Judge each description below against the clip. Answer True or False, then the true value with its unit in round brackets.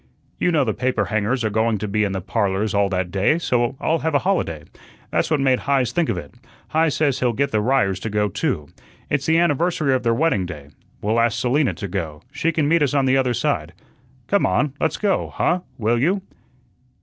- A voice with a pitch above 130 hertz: False (120 Hz)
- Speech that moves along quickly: True (220 wpm)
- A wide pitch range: True (6.4 semitones)